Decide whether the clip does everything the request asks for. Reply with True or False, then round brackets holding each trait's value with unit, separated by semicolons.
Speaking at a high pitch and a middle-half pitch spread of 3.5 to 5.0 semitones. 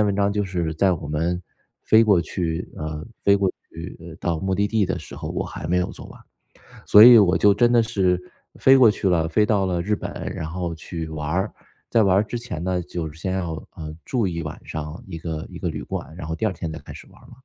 False (90 Hz; 3.9 semitones)